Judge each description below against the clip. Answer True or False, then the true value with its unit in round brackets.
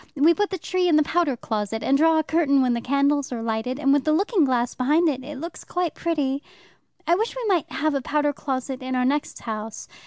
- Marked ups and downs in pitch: False (4.2 semitones)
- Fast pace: True (230 wpm)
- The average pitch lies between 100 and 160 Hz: False (285 Hz)